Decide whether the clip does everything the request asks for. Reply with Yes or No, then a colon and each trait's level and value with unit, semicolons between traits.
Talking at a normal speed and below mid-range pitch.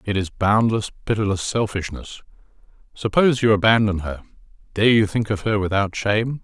Yes: average, 150 wpm; low, 105 Hz